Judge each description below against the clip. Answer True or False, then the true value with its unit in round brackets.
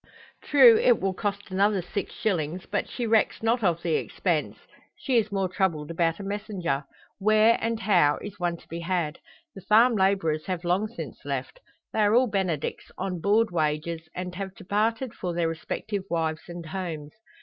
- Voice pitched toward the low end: False (190 Hz)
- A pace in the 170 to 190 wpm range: True (180 wpm)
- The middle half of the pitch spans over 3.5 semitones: True (4.0 semitones)